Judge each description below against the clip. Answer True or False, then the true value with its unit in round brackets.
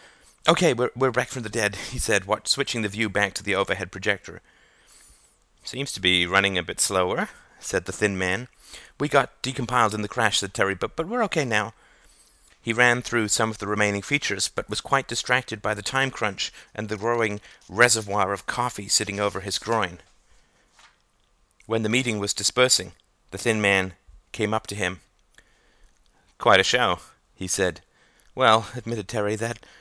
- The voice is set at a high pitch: False (105 Hz)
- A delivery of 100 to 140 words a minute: False (175 wpm)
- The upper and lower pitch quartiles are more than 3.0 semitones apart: True (3.4 semitones)